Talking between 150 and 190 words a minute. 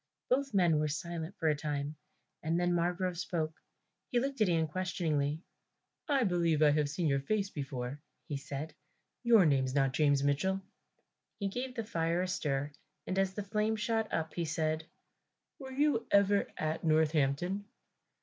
Yes: average, 165 wpm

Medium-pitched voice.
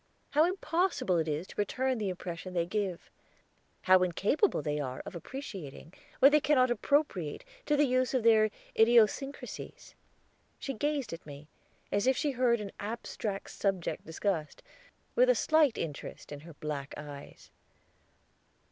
No: high, 210 Hz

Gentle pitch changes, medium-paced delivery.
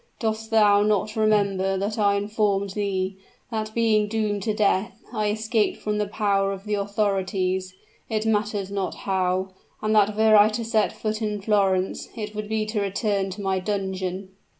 Yes: narrow, 1.7 semitones; average, 175 wpm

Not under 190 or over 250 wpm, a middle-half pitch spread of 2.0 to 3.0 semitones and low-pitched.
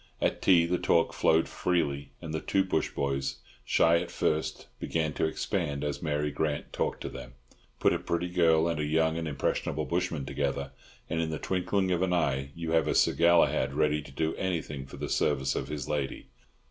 Yes: average, 200 wpm; average, 2.7 semitones; very low, 80 Hz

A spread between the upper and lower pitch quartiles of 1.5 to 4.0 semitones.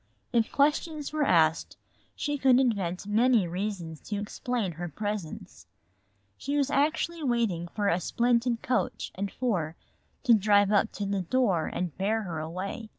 No: wide, 5.6 semitones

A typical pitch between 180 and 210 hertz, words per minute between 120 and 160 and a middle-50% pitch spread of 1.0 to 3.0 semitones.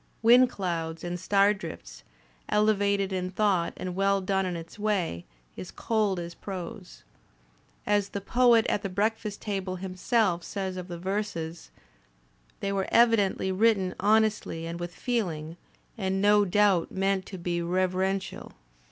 Yes: high, 190 Hz; average, 145 wpm; average, 2.7 semitones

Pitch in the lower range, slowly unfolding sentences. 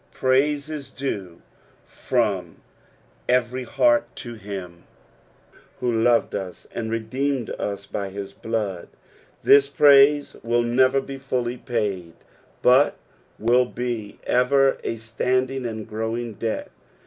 Yes: low, 120 Hz; slow, 115 wpm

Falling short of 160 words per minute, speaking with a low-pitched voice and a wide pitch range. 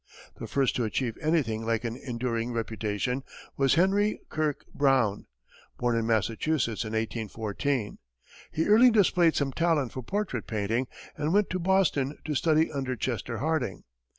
Yes: average, 150 wpm; low, 130 Hz; wide, 5.7 semitones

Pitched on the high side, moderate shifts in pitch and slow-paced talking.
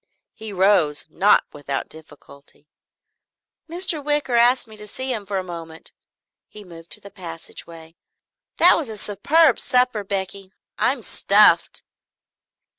No: high, 200 Hz; wide, 6.9 semitones; slow, 130 wpm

